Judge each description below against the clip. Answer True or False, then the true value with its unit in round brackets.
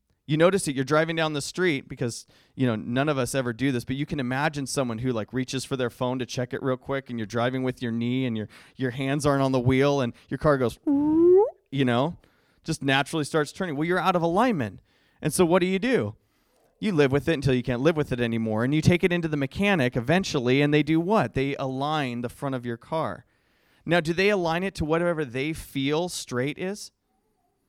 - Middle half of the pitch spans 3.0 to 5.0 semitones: True (4.2 semitones)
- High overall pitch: False (140 Hz)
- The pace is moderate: False (235 wpm)